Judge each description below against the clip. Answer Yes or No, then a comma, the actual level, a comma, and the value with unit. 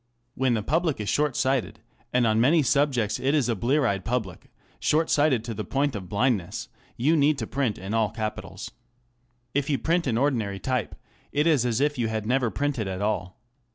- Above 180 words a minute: Yes, average, 200 wpm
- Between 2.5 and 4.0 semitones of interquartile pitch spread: No, average, 4.9 semitones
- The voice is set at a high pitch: No, low, 125 Hz